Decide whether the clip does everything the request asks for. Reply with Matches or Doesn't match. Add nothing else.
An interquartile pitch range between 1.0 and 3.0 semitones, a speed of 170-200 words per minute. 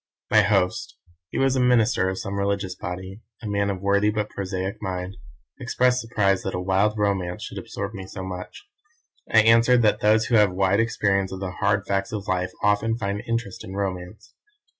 Matches